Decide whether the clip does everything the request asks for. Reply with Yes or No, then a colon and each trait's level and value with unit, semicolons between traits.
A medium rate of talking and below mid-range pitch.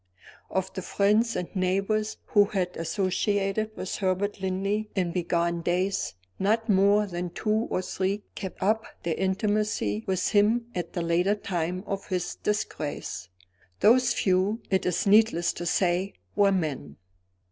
No: average, 145 wpm; high, 190 Hz